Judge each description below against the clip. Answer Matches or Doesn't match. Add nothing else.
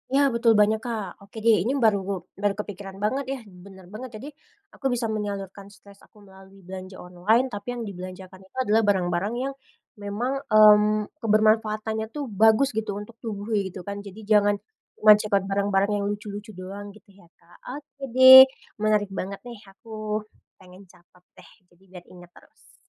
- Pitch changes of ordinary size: Doesn't match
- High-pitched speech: Matches